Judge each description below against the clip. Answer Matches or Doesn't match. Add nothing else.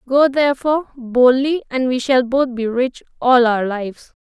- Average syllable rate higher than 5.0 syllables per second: Doesn't match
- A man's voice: Doesn't match